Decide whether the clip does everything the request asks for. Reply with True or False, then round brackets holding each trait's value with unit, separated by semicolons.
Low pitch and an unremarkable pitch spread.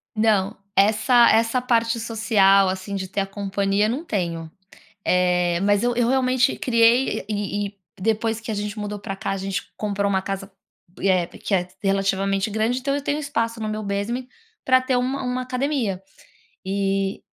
False (210 Hz; 3.3 semitones)